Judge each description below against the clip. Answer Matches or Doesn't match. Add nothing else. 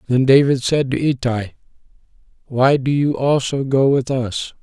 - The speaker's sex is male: Matches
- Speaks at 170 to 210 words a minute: Doesn't match